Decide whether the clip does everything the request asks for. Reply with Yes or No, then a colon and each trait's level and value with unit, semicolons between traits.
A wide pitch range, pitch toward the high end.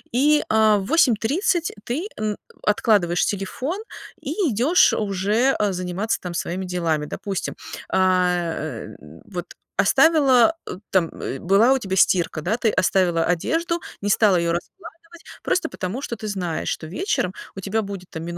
Yes: wide, 5.7 semitones; high, 200 Hz